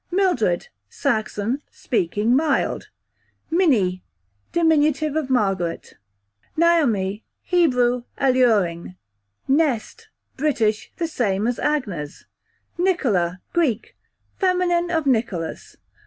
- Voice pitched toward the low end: No, high, 245 Hz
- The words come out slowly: Yes, slow, 85 wpm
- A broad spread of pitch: Yes, wide, 8.0 semitones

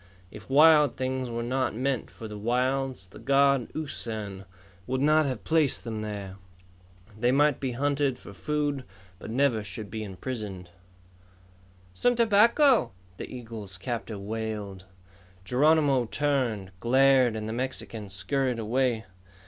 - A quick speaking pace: No, slow, 135 wpm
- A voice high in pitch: No, low, 125 Hz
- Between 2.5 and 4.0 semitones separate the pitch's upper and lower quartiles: No, average, 4.4 semitones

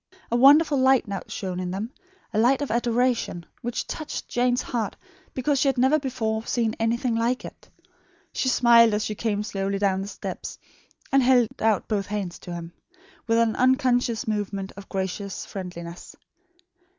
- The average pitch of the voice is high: Yes, high, 225 Hz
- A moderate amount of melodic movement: Yes, average, 4.1 semitones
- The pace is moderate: Yes, average, 170 wpm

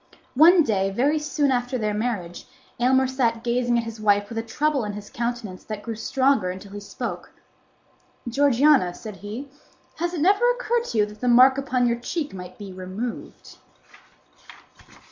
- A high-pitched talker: Yes, high, 240 Hz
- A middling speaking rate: Yes, average, 170 wpm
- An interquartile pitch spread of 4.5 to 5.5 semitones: Yes, average, 4.8 semitones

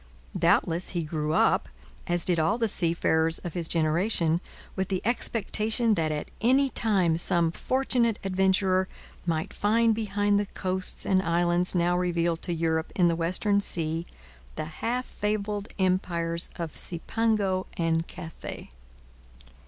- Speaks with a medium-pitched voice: Yes, medium, 180 Hz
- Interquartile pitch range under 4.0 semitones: Yes, average, 3.6 semitones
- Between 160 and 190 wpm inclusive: No, slow, 135 wpm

